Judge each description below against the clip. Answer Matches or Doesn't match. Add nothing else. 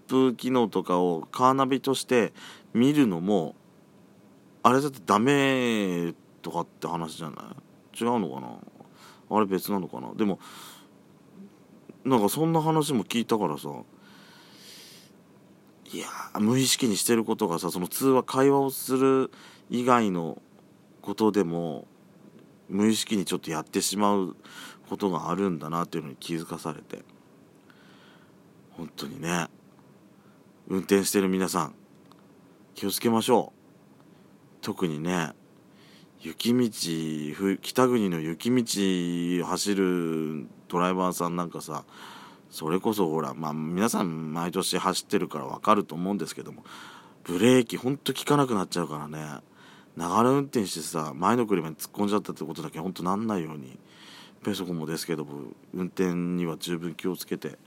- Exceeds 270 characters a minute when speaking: Matches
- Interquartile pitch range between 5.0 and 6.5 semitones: Matches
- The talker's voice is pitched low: Matches